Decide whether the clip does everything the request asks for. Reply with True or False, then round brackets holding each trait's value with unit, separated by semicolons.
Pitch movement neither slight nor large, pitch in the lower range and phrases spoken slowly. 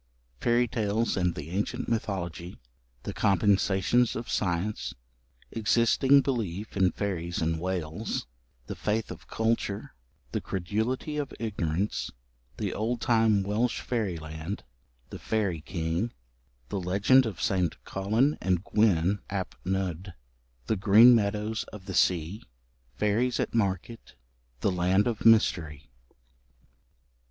True (3.9 semitones; 100 Hz; 120 wpm)